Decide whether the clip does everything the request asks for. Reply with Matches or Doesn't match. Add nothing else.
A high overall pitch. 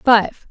Matches